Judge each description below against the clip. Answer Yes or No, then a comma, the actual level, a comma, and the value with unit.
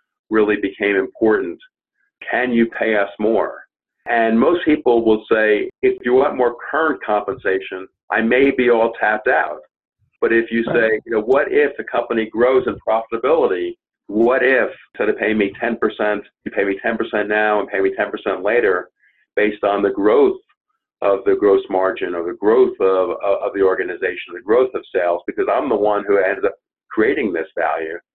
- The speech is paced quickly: No, average, 180 wpm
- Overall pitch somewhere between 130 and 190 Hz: No, low, 120 Hz